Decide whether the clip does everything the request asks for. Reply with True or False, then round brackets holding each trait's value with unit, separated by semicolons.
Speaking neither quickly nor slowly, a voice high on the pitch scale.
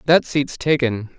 False (150 wpm; 135 Hz)